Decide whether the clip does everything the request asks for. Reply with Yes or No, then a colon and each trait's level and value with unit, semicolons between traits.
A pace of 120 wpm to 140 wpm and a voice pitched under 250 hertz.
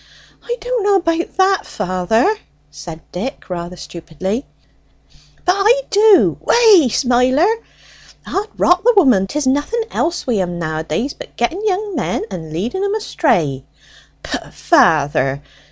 No: slow, 135 wpm; very high, 260 Hz